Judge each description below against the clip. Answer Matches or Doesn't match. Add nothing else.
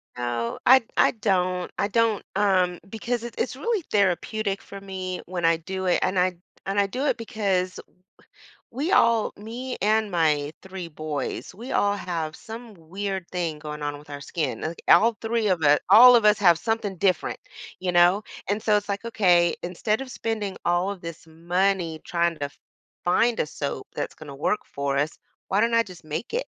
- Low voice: Doesn't match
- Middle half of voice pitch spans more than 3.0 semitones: Matches